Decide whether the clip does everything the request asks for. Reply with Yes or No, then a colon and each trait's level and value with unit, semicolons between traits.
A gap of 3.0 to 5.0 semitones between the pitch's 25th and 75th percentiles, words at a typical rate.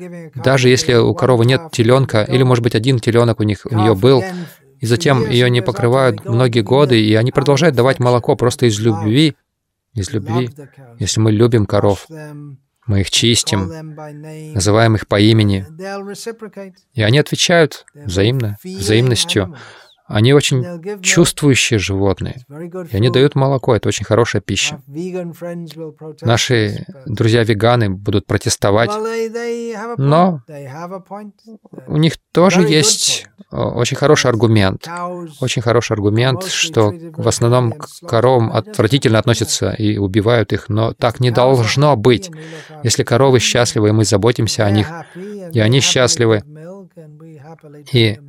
No: wide, 5.6 semitones; average, 130 wpm